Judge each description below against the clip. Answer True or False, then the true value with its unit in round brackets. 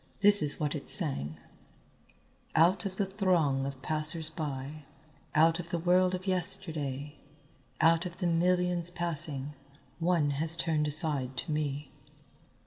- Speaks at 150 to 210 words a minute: False (135 wpm)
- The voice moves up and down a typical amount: True (3.3 semitones)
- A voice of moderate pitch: True (160 Hz)